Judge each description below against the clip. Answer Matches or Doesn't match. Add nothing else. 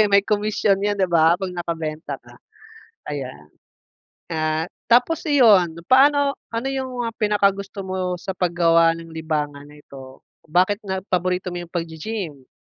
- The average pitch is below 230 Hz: Matches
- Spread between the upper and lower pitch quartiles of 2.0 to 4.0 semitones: Doesn't match